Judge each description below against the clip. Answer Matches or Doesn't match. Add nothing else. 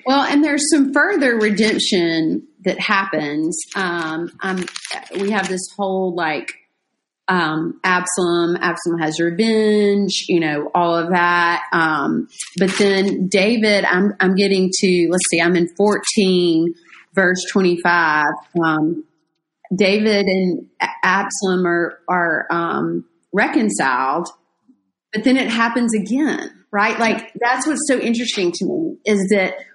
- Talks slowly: Matches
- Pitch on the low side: Doesn't match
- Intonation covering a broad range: Doesn't match